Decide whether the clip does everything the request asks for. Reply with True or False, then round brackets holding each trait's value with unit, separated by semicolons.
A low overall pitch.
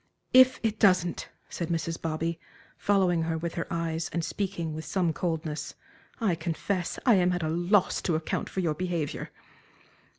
False (170 Hz)